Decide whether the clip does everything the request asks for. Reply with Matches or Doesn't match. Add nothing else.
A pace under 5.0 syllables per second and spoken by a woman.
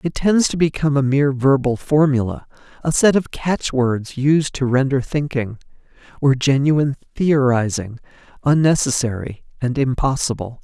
Doesn't match